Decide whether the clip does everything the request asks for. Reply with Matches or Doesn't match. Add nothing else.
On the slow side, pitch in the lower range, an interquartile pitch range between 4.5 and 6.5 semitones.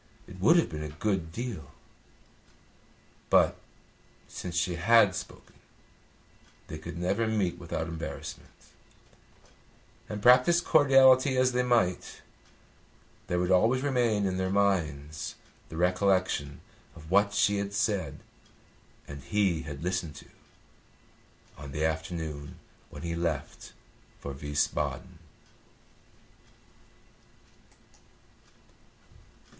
Matches